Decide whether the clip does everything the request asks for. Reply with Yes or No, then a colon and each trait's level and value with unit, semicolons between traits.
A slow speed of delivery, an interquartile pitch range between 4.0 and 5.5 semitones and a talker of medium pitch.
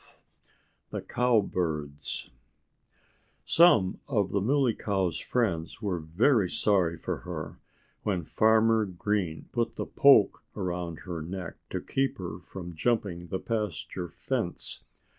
No: slow, 120 wpm; average, 4.4 semitones; very low, 95 Hz